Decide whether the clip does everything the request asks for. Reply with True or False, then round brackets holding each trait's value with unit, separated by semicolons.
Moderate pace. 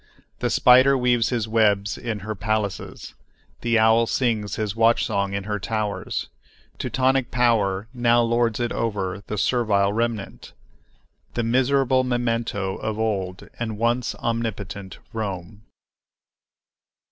False (125 wpm)